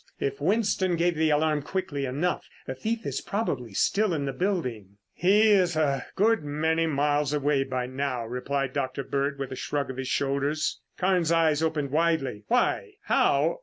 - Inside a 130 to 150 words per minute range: No, average, 165 wpm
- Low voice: No, medium, 150 Hz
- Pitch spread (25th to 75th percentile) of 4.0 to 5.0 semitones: Yes, average, 4.4 semitones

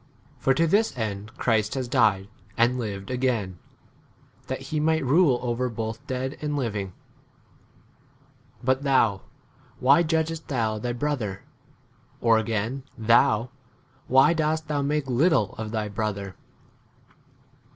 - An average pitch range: Yes, average, 4.7 semitones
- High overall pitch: No, low, 125 Hz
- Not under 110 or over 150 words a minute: Yes, average, 140 wpm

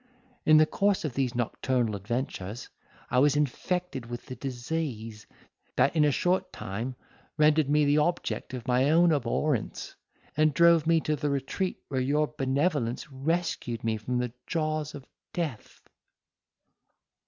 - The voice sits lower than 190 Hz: Yes, medium, 140 Hz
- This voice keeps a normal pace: Yes, average, 145 wpm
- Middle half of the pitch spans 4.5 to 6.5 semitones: No, average, 3.9 semitones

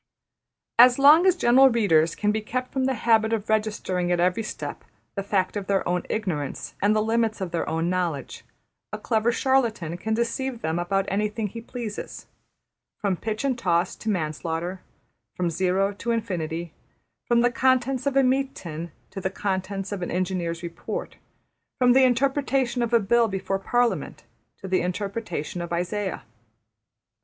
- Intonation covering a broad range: No, average, 4.9 semitones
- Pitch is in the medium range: No, high, 205 Hz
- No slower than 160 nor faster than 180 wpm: Yes, average, 165 wpm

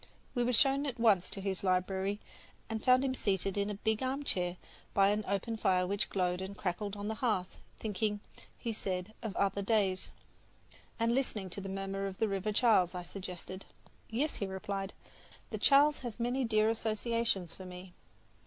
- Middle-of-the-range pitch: No, high, 200 Hz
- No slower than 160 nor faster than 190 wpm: Yes, average, 180 wpm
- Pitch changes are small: No, average, 3.2 semitones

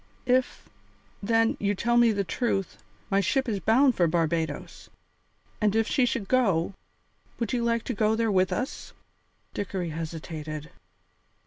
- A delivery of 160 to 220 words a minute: No, average, 145 wpm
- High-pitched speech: Yes, high, 205 Hz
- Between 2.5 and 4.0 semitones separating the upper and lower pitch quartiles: No, average, 5.3 semitones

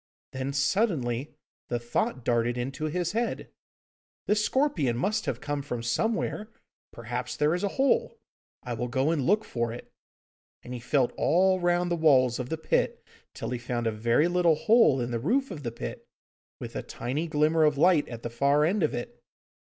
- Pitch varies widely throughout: Yes, wide, 6.5 semitones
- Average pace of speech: Yes, average, 190 wpm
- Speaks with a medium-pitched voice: Yes, medium, 145 Hz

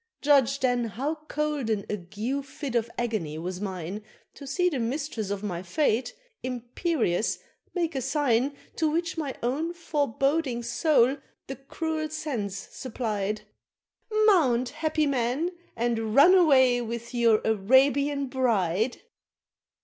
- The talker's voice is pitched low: No, very high, 255 Hz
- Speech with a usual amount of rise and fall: Yes, average, 4.8 semitones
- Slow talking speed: Yes, slow, 125 wpm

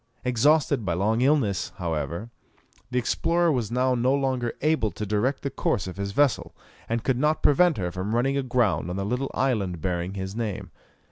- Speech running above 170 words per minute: Yes, average, 185 wpm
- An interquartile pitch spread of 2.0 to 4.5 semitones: No, wide, 5.5 semitones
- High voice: No, low, 120 Hz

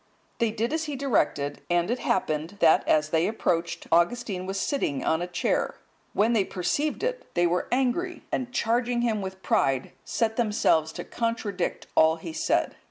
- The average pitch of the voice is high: Yes, high, 205 Hz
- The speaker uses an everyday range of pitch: No, wide, 6.1 semitones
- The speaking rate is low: No, average, 170 wpm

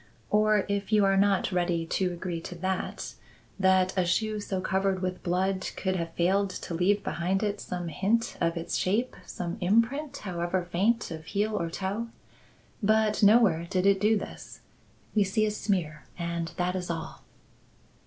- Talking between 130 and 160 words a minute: No, average, 170 wpm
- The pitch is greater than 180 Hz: Yes, high, 190 Hz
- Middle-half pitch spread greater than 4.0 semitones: No, average, 2.9 semitones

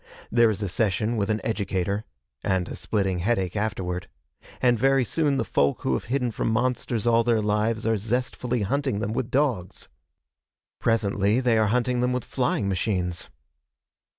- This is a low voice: Yes, low, 110 Hz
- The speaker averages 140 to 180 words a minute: Yes, average, 165 wpm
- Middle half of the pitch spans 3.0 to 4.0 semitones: Yes, average, 3.6 semitones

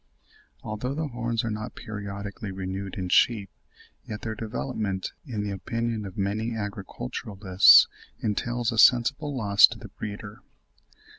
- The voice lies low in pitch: Yes, low, 105 Hz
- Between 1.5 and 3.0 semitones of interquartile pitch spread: Yes, average, 2.7 semitones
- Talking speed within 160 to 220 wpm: No, slow, 135 wpm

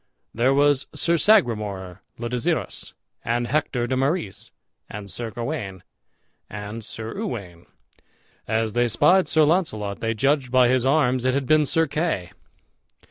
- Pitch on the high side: No, low, 120 Hz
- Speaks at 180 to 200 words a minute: No, average, 140 wpm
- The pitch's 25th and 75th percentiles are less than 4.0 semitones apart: No, average, 5.0 semitones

